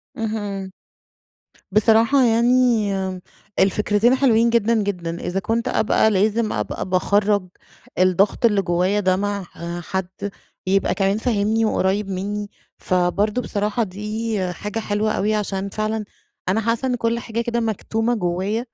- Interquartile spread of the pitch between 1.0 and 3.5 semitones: Yes, narrow, 2.6 semitones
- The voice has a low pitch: No, high, 210 Hz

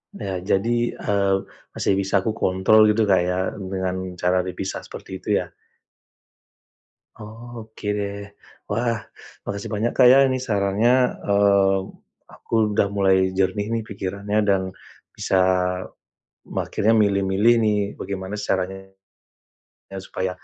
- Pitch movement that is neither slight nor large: No, narrow, 2.3 semitones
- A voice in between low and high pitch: No, low, 100 Hz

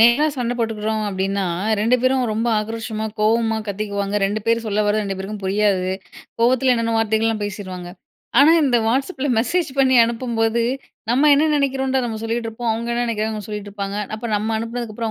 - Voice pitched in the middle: No, high, 225 Hz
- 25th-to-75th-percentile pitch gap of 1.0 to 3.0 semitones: Yes, narrow, 2.5 semitones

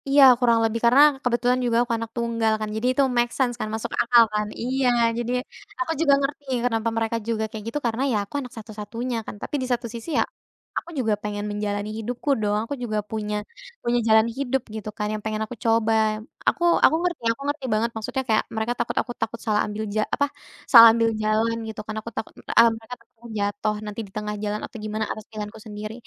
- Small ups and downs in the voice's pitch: Yes, narrow, 2.2 semitones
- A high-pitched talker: Yes, high, 225 Hz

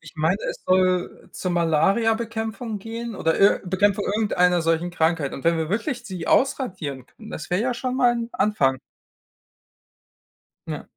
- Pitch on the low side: No, high, 190 Hz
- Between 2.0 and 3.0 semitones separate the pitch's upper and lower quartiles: No, average, 5.2 semitones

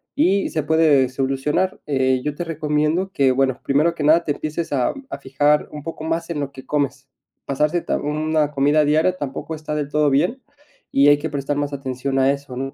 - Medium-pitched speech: Yes, medium, 150 Hz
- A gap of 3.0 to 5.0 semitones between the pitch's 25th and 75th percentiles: No, narrow, 2.4 semitones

